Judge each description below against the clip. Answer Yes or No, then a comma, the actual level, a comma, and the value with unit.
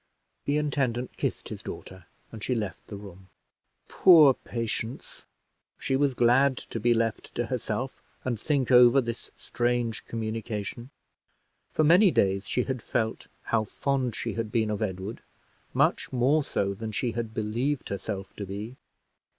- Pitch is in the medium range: No, low, 115 Hz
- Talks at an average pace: Yes, average, 150 wpm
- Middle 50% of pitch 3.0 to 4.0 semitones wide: Yes, average, 3.4 semitones